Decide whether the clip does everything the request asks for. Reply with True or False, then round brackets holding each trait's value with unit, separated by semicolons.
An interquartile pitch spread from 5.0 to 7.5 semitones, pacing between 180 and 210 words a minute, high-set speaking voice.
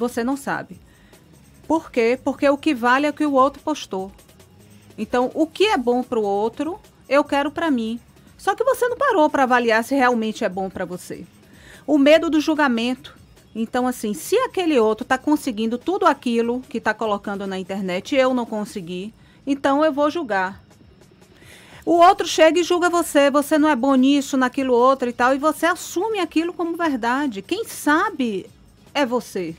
True (5.4 semitones; 185 wpm; 270 Hz)